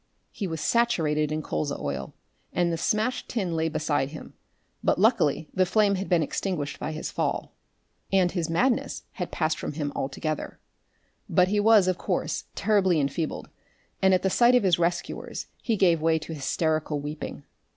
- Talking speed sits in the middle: Yes, average, 170 wpm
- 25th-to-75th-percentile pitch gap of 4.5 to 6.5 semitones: No, average, 4.0 semitones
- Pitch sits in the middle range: Yes, medium, 170 Hz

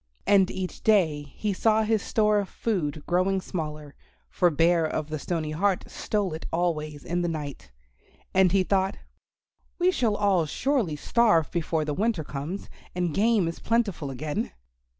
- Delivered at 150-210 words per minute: Yes, average, 160 wpm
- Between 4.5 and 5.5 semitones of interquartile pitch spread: Yes, average, 4.8 semitones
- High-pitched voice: No, medium, 175 Hz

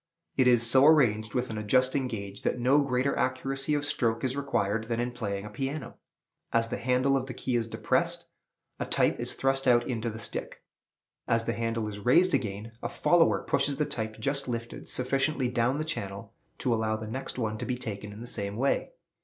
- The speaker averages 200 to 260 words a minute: Yes, fast, 205 wpm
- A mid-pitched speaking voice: No, low, 120 Hz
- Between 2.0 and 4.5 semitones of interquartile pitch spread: Yes, average, 3.4 semitones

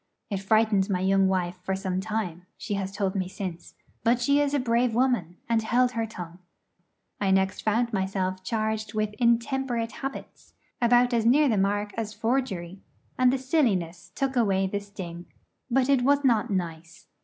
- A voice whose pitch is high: Yes, high, 215 Hz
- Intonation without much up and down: No, average, 4.2 semitones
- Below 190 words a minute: Yes, average, 175 wpm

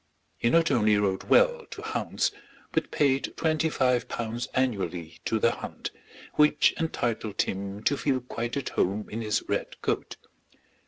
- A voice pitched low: Yes, low, 120 Hz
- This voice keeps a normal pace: Yes, average, 155 wpm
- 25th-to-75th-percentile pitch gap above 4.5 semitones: Yes, average, 5.1 semitones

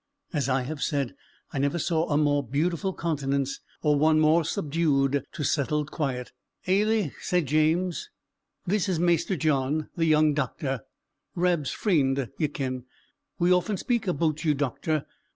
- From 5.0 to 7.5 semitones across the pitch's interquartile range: No, average, 3.4 semitones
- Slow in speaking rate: No, average, 150 wpm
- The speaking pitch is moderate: Yes, medium, 155 Hz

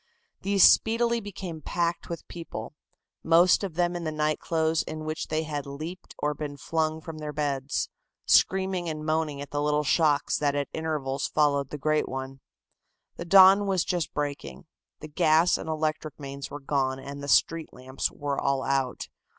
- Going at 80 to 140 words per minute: No, average, 175 wpm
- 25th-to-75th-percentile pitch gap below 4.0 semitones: Yes, average, 2.8 semitones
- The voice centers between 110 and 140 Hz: No, medium, 155 Hz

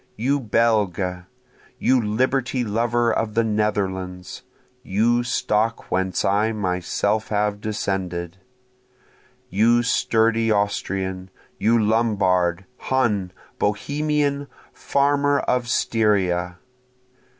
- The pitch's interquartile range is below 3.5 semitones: No, average, 3.8 semitones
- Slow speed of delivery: Yes, slow, 85 wpm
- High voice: No, low, 105 Hz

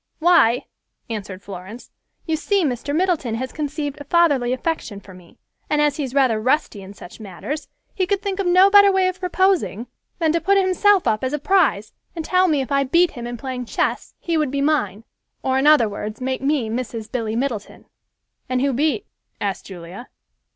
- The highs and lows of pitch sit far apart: Yes, wide, 6.9 semitones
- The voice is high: Yes, very high, 275 Hz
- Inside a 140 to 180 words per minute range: No, average, 200 wpm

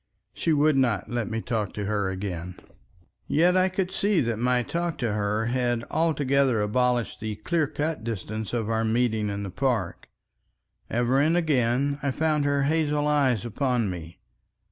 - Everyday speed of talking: Yes, average, 165 wpm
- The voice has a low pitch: Yes, low, 125 Hz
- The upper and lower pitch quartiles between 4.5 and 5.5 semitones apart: Yes, average, 5.2 semitones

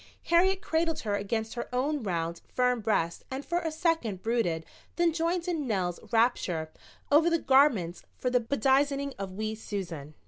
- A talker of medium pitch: No, high, 245 Hz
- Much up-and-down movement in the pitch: Yes, wide, 7.8 semitones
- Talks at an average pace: Yes, average, 165 wpm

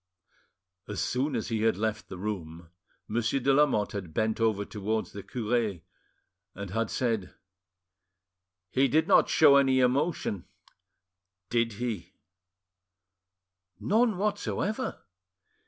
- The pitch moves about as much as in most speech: Yes, average, 4.8 semitones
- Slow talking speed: Yes, slow, 110 wpm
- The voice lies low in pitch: Yes, low, 115 Hz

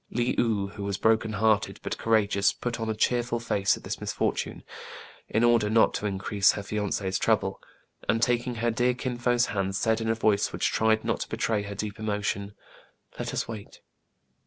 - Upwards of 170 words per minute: Yes, average, 190 wpm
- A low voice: Yes, low, 110 Hz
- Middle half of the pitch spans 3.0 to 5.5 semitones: No, narrow, 2.4 semitones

